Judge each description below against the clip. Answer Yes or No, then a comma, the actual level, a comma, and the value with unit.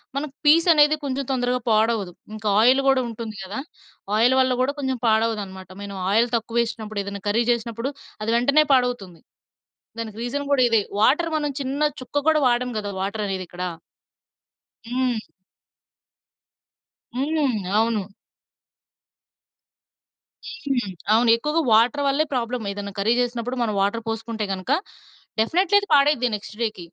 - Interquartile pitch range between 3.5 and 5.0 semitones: Yes, average, 3.9 semitones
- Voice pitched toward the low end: No, high, 235 Hz